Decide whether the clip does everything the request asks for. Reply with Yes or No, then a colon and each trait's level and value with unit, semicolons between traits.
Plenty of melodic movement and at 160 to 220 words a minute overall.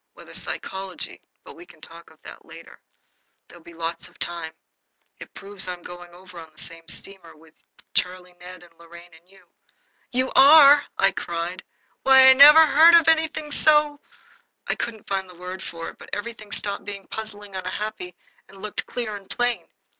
Yes: wide, 5.7 semitones; average, 185 wpm